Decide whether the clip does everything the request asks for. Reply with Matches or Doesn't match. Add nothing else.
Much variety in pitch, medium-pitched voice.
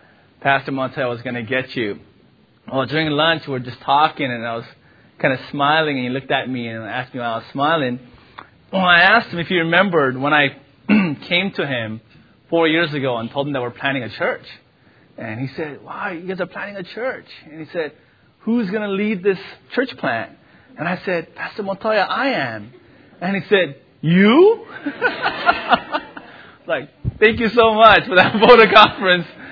Matches